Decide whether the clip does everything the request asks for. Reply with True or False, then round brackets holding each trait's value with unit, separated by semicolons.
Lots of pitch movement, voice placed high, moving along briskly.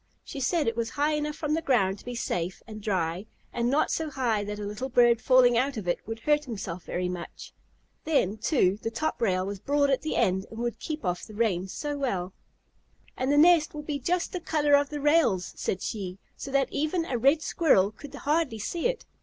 True (6.4 semitones; 245 Hz; 225 wpm)